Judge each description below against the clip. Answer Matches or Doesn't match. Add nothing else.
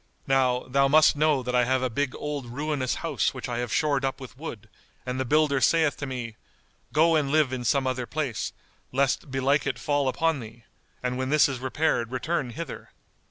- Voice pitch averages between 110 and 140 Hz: Matches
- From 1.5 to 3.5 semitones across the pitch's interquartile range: Matches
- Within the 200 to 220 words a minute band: Matches